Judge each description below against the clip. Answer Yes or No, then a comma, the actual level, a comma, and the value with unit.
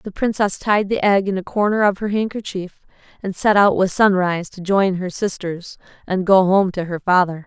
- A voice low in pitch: No, high, 190 Hz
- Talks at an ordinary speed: No, fast, 210 wpm